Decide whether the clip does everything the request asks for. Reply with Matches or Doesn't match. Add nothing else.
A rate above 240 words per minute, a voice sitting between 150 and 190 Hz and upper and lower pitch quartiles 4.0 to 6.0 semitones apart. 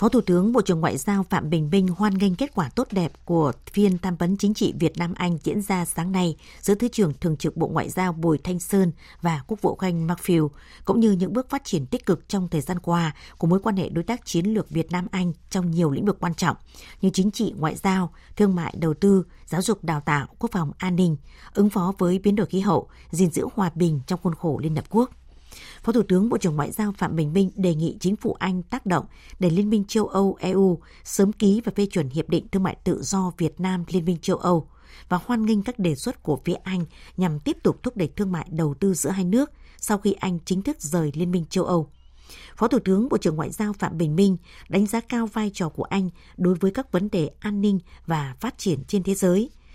Doesn't match